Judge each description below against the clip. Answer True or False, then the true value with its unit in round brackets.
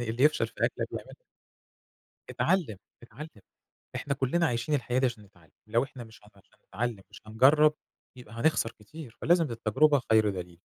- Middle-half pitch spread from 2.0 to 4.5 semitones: False (5.4 semitones)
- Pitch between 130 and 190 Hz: False (120 Hz)